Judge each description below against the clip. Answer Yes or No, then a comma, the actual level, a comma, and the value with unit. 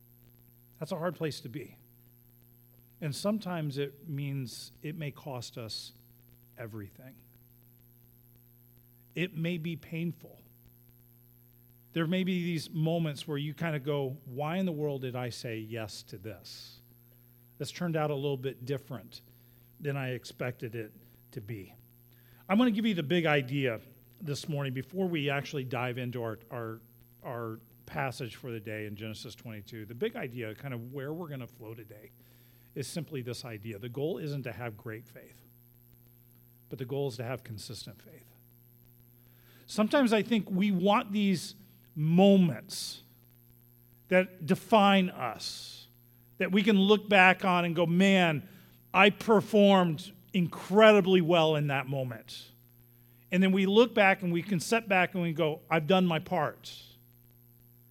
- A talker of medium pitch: No, low, 125 Hz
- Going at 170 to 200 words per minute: No, average, 155 wpm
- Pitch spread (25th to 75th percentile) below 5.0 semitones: No, wide, 5.6 semitones